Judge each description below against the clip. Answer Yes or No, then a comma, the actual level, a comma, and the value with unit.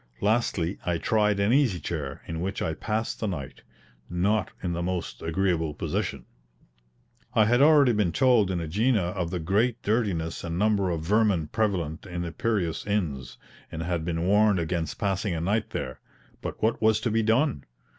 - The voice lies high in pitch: No, very low, 95 Hz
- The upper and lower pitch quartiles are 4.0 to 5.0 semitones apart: Yes, average, 4.6 semitones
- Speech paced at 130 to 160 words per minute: No, average, 175 wpm